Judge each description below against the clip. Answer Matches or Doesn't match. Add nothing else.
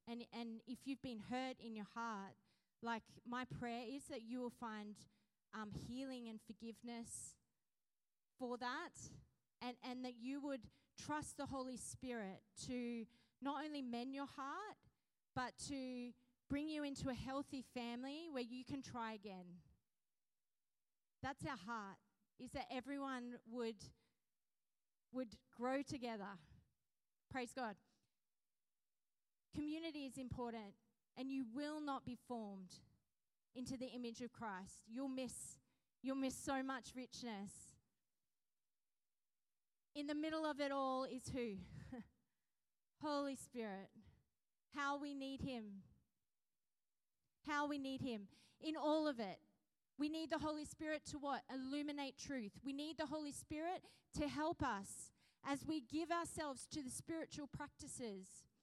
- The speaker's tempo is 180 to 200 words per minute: Doesn't match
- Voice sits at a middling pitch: Doesn't match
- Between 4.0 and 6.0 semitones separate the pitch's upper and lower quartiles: Doesn't match